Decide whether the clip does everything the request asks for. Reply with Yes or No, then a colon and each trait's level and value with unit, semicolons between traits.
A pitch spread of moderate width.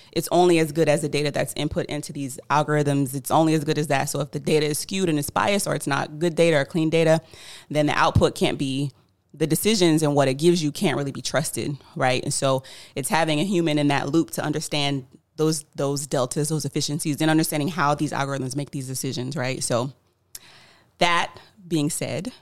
No: narrow, 2.3 semitones